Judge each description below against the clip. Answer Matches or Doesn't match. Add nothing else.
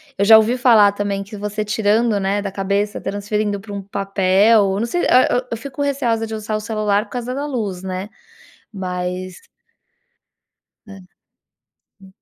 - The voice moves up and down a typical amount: Doesn't match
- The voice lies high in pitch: Matches